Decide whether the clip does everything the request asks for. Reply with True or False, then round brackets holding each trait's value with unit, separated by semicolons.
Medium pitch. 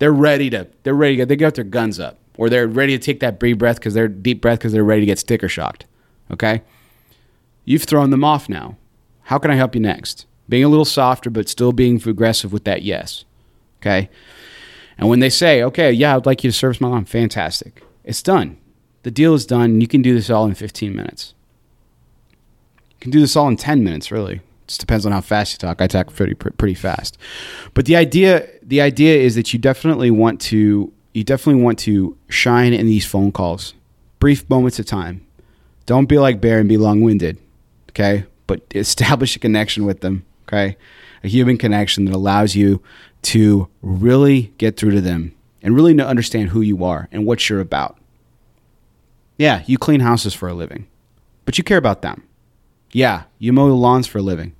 False (115 Hz)